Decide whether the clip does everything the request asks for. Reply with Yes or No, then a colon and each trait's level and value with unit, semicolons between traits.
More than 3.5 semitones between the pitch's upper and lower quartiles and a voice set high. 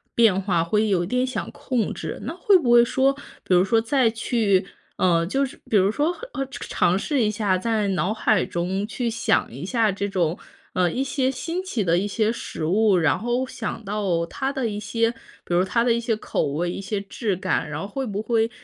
Yes: average, 4.2 semitones; high, 215 Hz